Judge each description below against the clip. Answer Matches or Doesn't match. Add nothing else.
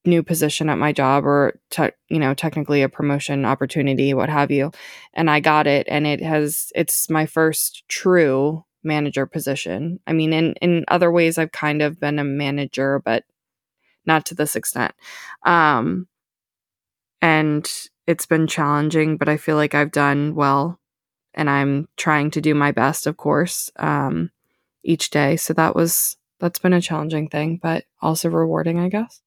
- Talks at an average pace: Matches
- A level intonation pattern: Matches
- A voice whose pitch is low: Doesn't match